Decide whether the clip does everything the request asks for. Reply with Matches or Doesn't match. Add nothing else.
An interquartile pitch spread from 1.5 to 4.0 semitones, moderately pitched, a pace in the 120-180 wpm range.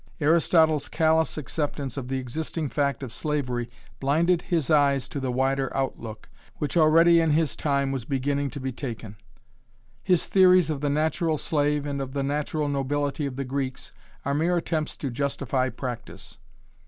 Matches